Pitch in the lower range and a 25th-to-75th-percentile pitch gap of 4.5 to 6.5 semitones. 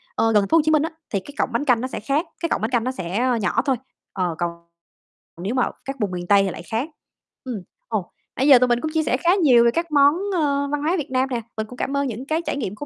No: very high, 255 Hz; average, 5.2 semitones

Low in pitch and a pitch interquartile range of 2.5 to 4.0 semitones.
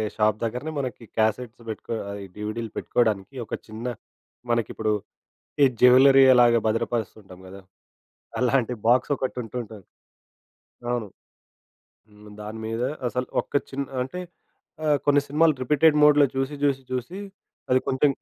Yes: low, 120 Hz; average, 3.6 semitones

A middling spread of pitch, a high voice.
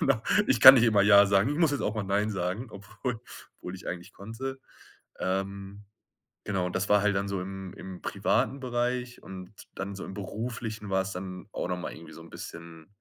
No: average, 3.1 semitones; low, 100 Hz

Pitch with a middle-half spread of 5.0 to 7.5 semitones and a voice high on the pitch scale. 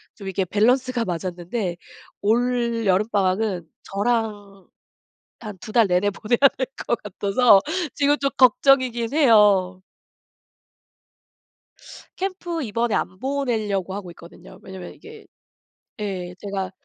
No: average, 4.4 semitones; high, 210 Hz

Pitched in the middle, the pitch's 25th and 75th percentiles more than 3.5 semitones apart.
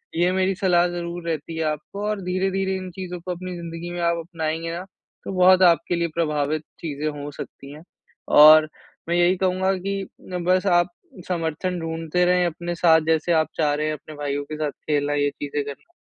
No: medium, 170 Hz; average, 2.8 semitones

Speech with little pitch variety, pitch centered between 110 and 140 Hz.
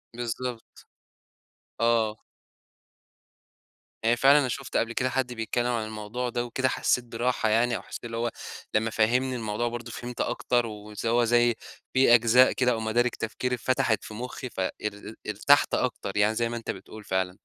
Yes: narrow, 2.1 semitones; low, 120 Hz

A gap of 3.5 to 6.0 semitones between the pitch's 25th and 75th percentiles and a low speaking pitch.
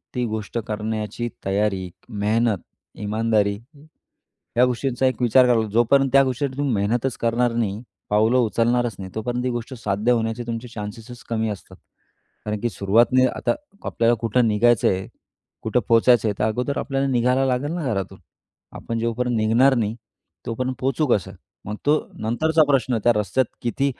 No: average, 2.8 semitones; low, 115 Hz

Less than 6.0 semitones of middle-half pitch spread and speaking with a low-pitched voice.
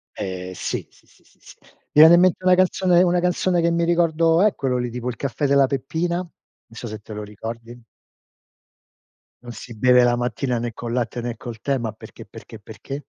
No: wide, 6.3 semitones; low, 125 Hz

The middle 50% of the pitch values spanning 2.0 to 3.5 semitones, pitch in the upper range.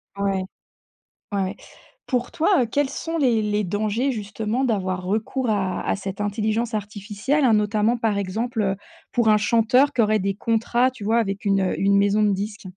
Yes: average, 2.9 semitones; high, 215 Hz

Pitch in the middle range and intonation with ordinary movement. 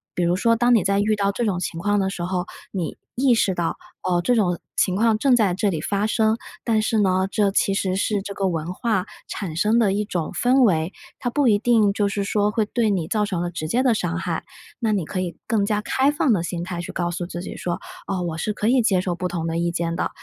No: high, 195 Hz; average, 3.7 semitones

